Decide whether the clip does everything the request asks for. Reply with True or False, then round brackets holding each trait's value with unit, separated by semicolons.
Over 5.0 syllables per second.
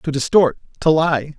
False (4.6 syllables/s)